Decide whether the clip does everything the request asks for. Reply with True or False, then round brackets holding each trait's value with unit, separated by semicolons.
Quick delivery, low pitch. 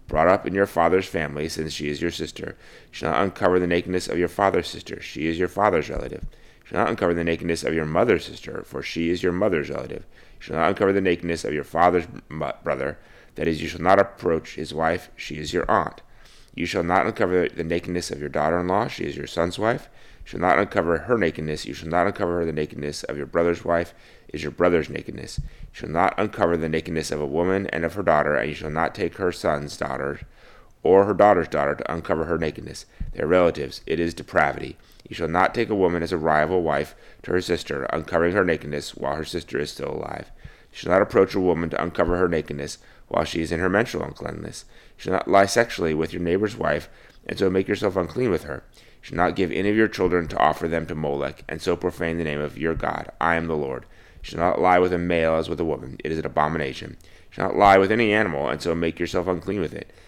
True (245 wpm; 85 Hz)